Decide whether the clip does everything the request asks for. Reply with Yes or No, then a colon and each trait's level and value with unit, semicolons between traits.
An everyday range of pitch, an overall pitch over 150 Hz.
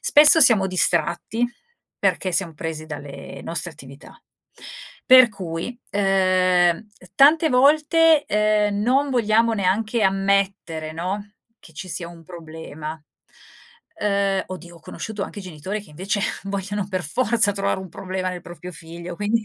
Yes: average, 3.9 semitones; high, 190 Hz